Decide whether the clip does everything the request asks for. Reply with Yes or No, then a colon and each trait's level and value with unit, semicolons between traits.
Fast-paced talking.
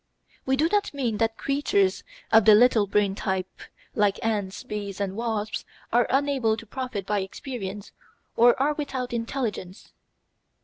No: average, 145 wpm